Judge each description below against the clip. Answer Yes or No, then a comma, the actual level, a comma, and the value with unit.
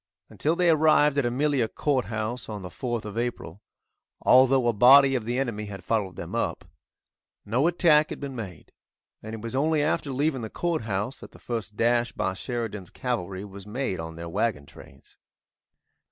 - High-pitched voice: No, low, 120 Hz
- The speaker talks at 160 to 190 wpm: Yes, average, 175 wpm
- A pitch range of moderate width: Yes, average, 4.7 semitones